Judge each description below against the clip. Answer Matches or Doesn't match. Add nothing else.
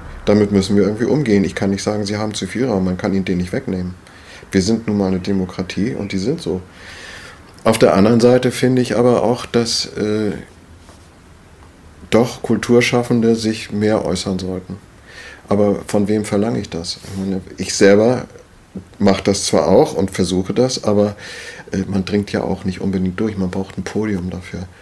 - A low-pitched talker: Matches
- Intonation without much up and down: Matches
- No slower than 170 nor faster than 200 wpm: Matches